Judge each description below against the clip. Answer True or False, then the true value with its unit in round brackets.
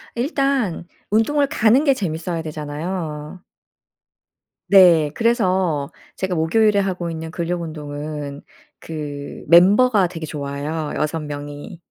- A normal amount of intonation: True (5.0 semitones)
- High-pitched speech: False (170 Hz)